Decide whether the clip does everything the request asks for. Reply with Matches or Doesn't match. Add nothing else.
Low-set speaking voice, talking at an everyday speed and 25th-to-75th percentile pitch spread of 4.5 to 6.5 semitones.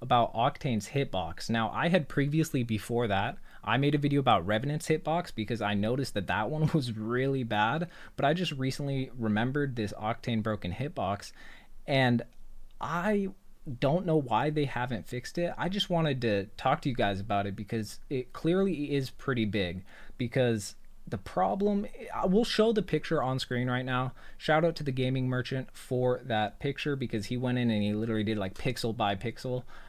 Matches